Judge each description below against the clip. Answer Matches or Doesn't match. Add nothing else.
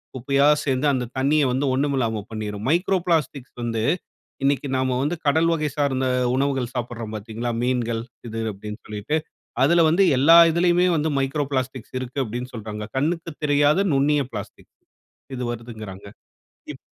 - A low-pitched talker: Matches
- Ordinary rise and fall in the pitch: Matches